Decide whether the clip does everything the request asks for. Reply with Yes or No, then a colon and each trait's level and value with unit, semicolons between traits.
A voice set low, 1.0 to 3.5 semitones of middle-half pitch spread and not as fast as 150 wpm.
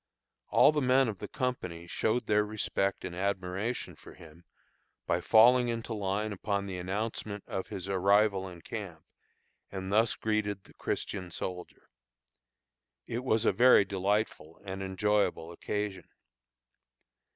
Yes: low, 100 Hz; average, 2.7 semitones; slow, 135 wpm